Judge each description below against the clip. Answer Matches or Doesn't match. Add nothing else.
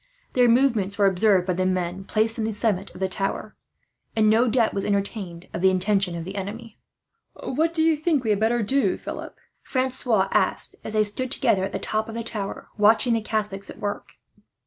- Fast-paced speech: Matches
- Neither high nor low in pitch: Doesn't match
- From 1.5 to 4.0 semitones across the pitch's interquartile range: Matches